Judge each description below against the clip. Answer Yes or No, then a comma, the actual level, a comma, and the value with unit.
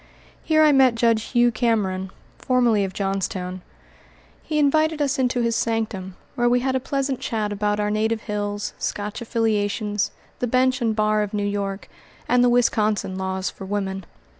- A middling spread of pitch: Yes, average, 3.2 semitones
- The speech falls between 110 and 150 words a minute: No, average, 165 wpm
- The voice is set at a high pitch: Yes, high, 220 Hz